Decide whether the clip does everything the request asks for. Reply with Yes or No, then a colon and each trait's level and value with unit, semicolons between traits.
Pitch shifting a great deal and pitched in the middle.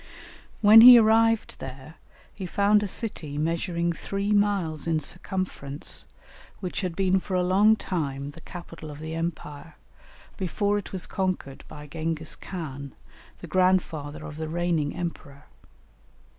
No: average, 4.1 semitones; medium, 170 Hz